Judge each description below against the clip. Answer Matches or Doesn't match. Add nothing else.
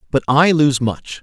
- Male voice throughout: Matches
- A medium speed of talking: Matches